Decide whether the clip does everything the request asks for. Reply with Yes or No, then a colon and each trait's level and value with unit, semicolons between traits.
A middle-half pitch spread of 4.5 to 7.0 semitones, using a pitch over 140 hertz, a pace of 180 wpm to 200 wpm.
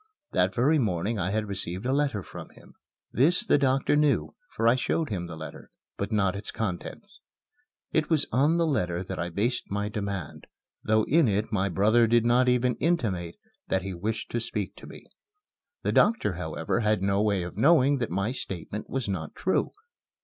No: average, 5.3 semitones; low, 110 Hz; average, 190 wpm